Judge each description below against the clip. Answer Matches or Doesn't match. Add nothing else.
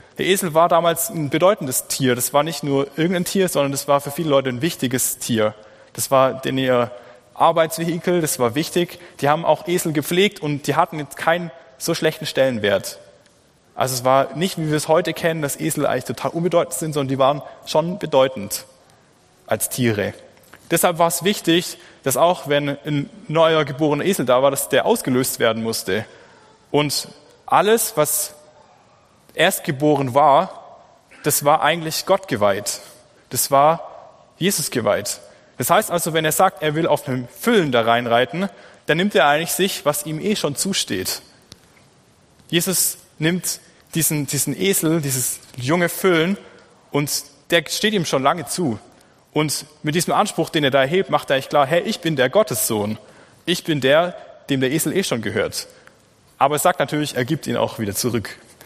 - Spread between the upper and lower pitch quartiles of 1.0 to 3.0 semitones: Doesn't match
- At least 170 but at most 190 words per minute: Matches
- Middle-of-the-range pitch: Matches